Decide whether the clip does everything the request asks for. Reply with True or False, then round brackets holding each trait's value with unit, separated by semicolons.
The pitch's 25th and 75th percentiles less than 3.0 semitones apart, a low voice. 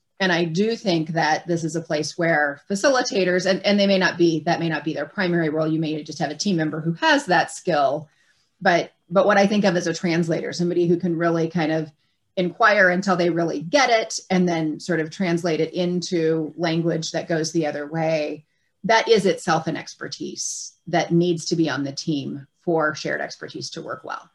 False (2.4 semitones; 170 Hz)